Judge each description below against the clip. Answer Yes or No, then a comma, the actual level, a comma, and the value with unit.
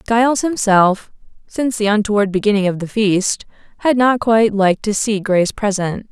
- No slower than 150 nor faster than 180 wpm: Yes, average, 165 wpm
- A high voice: Yes, high, 210 Hz